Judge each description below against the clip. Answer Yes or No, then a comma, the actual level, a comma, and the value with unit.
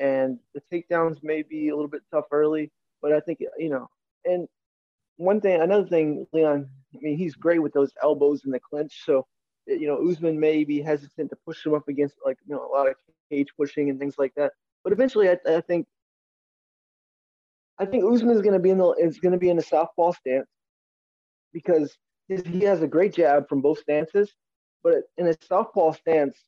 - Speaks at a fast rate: Yes, fast, 210 wpm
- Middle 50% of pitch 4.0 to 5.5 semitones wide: No, average, 3.3 semitones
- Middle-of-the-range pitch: Yes, medium, 155 Hz